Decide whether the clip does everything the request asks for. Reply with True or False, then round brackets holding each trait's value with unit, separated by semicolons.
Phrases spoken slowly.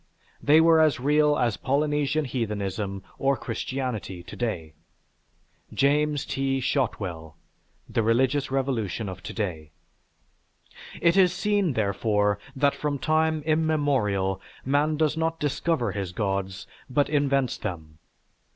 True (120 wpm)